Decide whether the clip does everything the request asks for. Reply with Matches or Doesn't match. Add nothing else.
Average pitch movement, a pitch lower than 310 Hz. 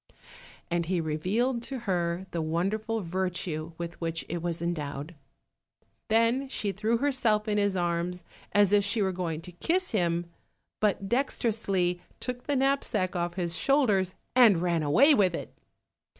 Matches